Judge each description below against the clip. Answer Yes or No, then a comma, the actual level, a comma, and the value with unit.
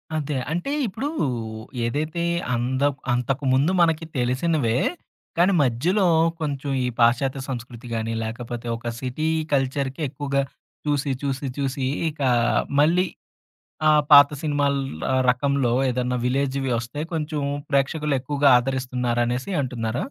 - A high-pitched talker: No, low, 135 Hz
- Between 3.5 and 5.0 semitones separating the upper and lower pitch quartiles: No, average, 2.9 semitones